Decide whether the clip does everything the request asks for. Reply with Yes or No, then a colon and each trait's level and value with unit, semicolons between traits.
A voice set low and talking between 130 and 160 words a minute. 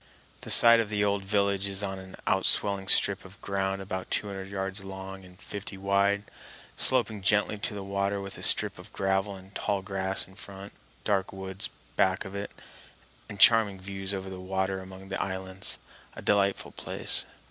No: very low, 95 Hz; average, 180 wpm